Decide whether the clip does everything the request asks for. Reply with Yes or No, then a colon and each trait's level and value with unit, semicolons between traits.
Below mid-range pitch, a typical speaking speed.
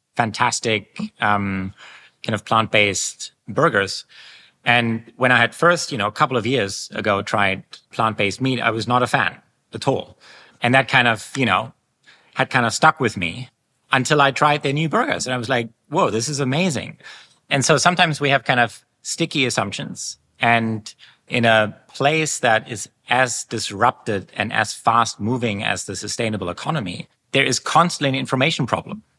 Yes: low, 120 Hz; average, 175 wpm